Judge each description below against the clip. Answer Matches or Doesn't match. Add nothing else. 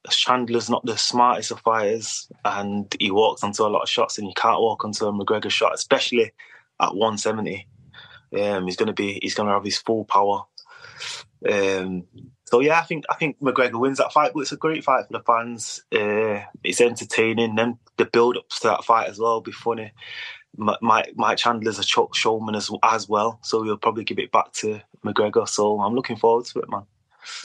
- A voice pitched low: Matches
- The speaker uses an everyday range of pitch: Matches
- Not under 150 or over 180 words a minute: Doesn't match